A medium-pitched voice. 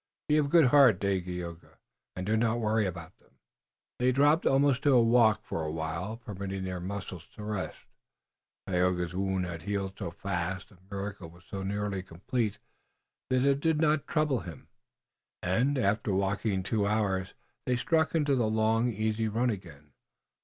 No: low, 100 Hz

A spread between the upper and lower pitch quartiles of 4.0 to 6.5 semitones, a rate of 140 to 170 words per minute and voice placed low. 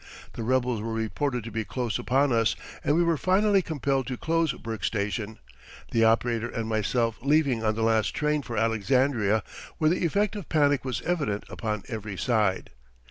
No: average, 4.5 semitones; average, 180 wpm; low, 120 Hz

